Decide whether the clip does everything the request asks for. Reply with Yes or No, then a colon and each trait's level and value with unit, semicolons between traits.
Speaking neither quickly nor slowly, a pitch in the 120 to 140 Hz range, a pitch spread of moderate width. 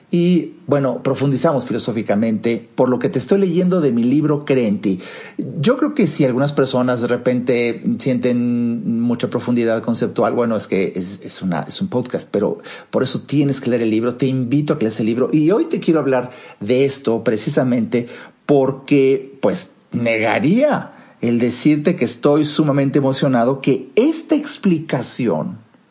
Yes: average, 165 wpm; low, 135 Hz; average, 4.0 semitones